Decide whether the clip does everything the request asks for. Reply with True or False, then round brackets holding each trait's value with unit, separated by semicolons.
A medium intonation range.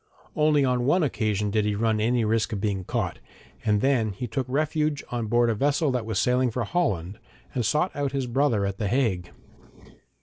True (4.6 semitones)